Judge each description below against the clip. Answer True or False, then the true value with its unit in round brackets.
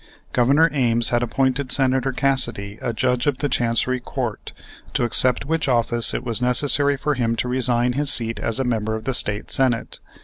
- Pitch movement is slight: True (2.3 semitones)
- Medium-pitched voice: False (125 Hz)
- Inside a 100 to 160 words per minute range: False (190 wpm)